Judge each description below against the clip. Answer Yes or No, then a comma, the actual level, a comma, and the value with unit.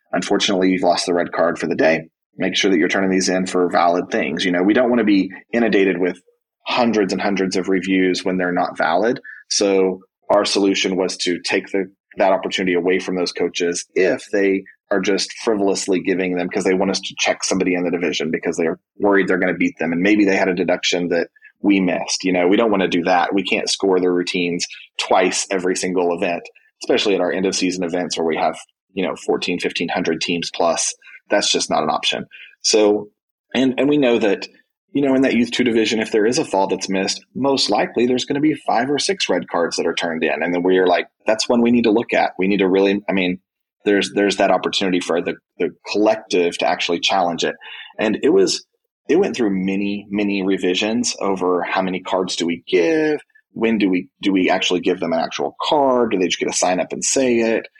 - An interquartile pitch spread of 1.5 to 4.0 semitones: Yes, average, 3.4 semitones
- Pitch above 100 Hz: No, very low, 95 Hz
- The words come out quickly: Yes, fast, 235 wpm